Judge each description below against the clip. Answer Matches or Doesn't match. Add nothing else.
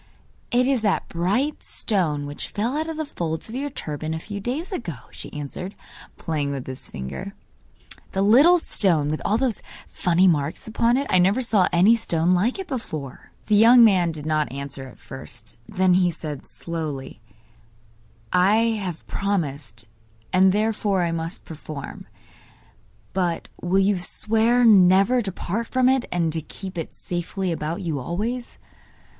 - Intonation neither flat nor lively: Doesn't match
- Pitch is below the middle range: Doesn't match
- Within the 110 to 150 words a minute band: Doesn't match